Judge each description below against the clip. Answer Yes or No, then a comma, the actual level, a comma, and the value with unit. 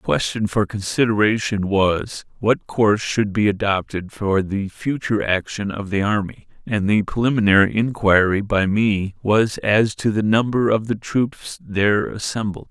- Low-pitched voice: Yes, low, 105 Hz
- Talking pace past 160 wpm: No, average, 155 wpm